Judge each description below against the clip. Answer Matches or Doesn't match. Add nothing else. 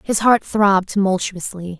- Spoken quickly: Doesn't match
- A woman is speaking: Matches